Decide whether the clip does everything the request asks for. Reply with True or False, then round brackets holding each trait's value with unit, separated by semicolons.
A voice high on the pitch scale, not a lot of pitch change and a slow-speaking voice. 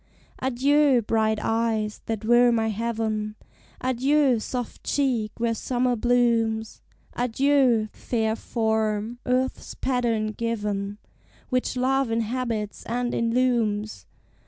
True (230 Hz; 2.3 semitones; 100 wpm)